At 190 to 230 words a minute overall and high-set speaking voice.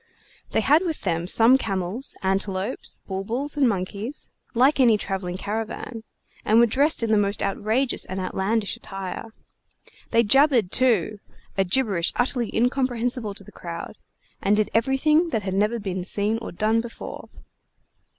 No: average, 150 wpm; high, 220 Hz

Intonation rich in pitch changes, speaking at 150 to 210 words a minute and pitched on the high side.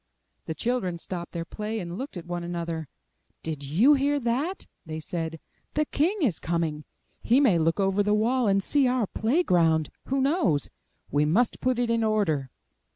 Yes: wide, 7.2 semitones; average, 185 wpm; high, 195 Hz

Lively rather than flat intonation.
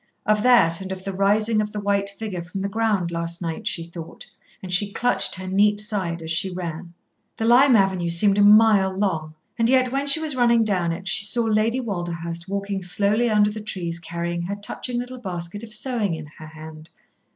No: average, 4.0 semitones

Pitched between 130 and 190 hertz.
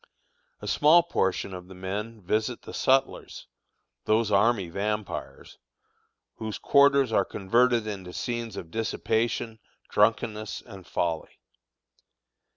No: low, 110 Hz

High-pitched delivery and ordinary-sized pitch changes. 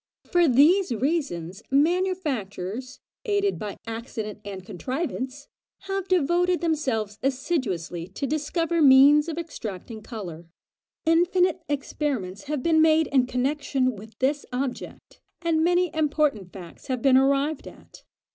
No: very high, 275 Hz; wide, 6.5 semitones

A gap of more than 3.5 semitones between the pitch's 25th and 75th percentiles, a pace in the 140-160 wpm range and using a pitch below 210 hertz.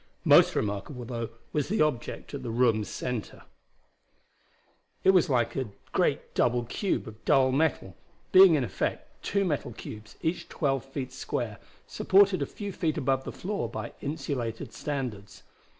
Yes: average, 5.0 semitones; average, 150 wpm; low, 135 Hz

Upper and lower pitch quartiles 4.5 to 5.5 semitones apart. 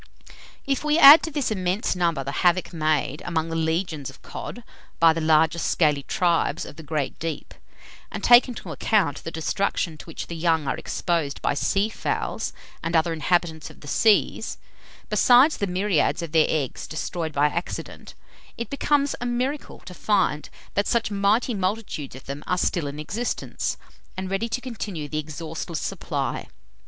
Yes: average, 5.1 semitones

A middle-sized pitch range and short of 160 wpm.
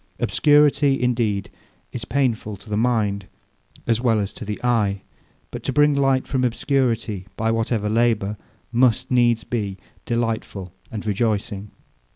Yes: average, 3.0 semitones; average, 140 wpm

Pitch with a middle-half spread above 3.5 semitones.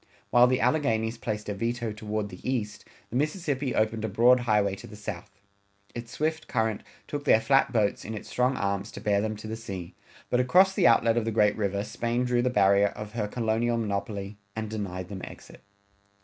No: average, 2.9 semitones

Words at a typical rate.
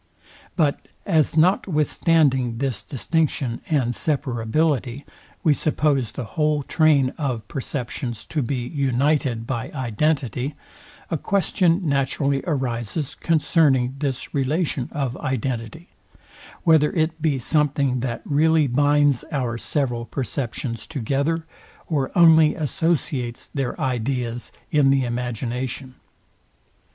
No: slow, 105 wpm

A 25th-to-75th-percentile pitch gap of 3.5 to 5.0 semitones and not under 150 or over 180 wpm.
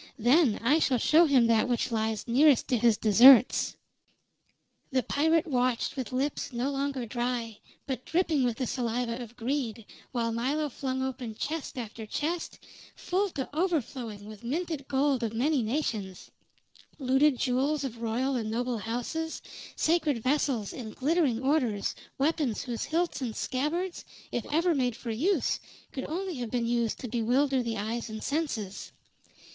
Yes: average, 4.1 semitones; average, 155 wpm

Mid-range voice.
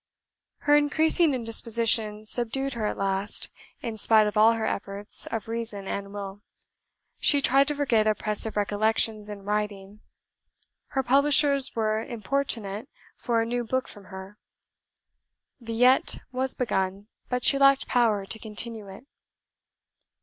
No: high, 225 Hz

